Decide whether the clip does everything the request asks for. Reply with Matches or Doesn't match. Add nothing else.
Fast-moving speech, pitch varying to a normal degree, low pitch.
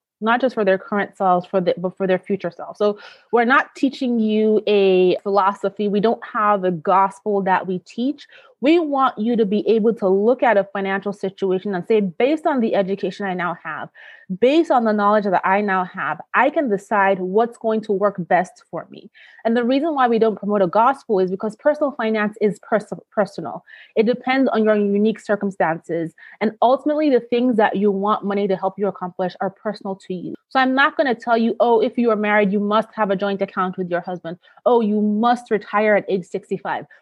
Doesn't match